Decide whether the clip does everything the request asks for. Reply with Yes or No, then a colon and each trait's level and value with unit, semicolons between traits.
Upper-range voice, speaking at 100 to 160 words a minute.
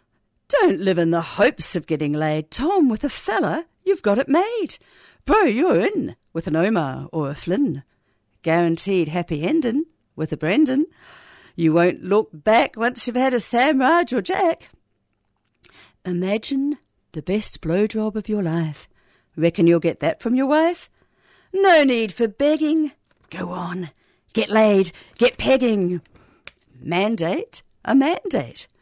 Yes: high, 205 Hz; average, 145 wpm